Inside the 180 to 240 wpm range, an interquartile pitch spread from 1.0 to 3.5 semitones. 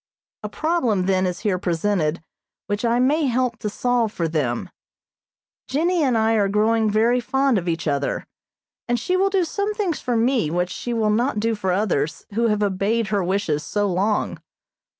No: average, 185 wpm; average, 4.8 semitones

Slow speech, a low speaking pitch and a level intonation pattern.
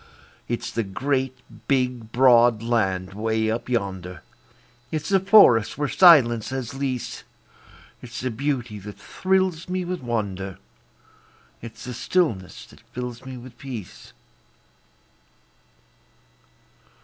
No: slow, 115 wpm; low, 120 Hz; average, 3.7 semitones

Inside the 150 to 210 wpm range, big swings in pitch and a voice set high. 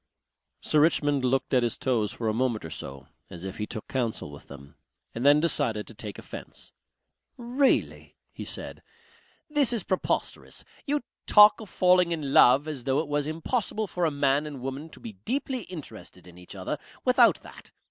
No: average, 185 wpm; wide, 7.8 semitones; medium, 145 Hz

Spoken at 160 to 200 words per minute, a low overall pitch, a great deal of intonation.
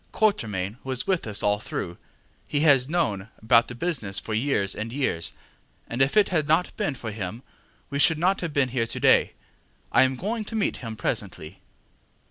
Yes: average, 190 wpm; low, 130 Hz; wide, 7.0 semitones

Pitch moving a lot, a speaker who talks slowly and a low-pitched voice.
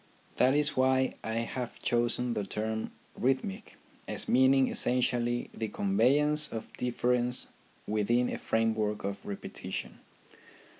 No: average, 2.8 semitones; slow, 120 wpm; low, 120 Hz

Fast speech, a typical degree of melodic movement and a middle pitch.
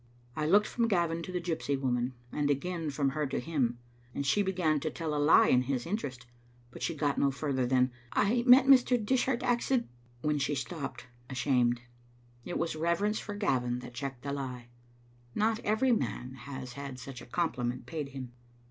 No: fast, 210 wpm; wide, 6.0 semitones; medium, 145 Hz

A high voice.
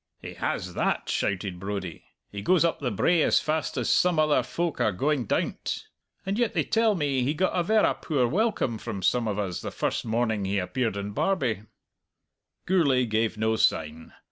No: low, 125 Hz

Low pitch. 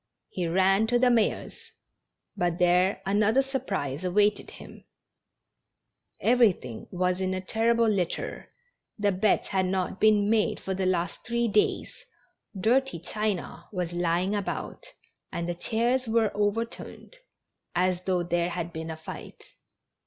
No: high, 195 Hz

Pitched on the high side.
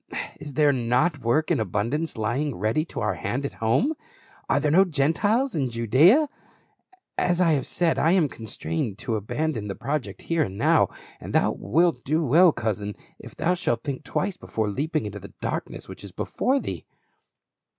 No: medium, 145 Hz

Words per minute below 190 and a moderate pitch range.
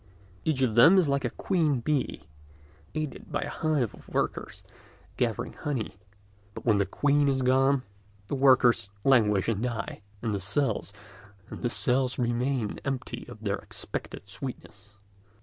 Yes: average, 140 wpm; average, 4.8 semitones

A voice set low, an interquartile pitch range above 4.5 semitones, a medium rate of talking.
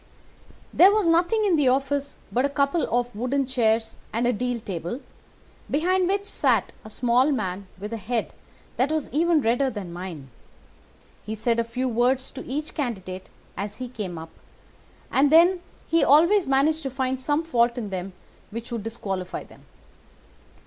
No: very high, 250 Hz; average, 5.1 semitones; average, 170 wpm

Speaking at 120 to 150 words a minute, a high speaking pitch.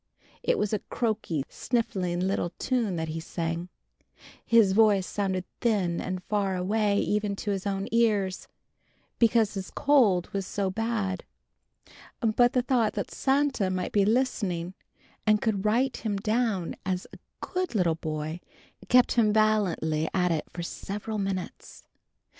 Yes: average, 145 wpm; high, 200 Hz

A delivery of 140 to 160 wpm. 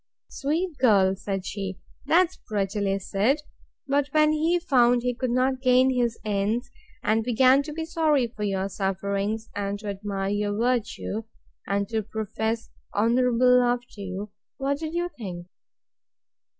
Yes: average, 150 wpm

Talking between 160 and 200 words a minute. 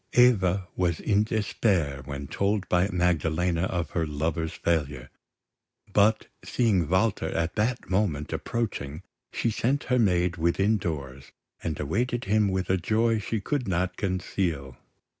No: average, 140 wpm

